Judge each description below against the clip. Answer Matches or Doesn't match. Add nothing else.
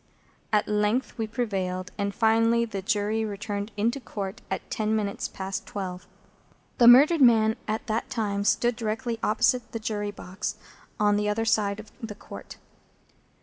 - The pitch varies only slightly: Matches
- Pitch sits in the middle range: Doesn't match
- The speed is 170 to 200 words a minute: Doesn't match